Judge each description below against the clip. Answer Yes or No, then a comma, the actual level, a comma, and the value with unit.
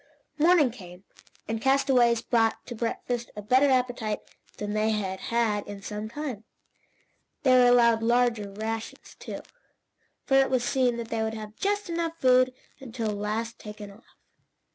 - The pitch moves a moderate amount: Yes, average, 3.0 semitones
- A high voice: Yes, high, 230 Hz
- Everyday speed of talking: Yes, average, 160 wpm